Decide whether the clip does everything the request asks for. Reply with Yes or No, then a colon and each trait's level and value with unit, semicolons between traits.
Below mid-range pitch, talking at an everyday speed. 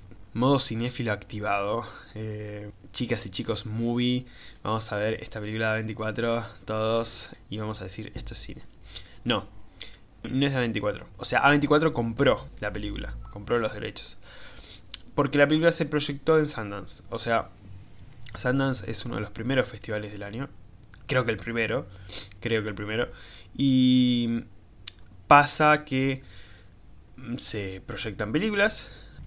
Yes: low, 110 Hz; average, 140 wpm